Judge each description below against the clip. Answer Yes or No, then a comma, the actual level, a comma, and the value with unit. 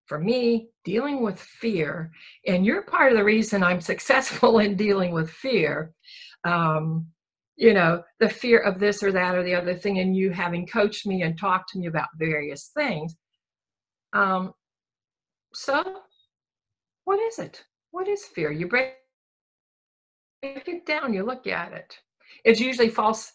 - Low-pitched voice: No, high, 195 Hz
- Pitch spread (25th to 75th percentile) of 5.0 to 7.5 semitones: Yes, wide, 5.5 semitones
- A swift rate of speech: No, average, 155 wpm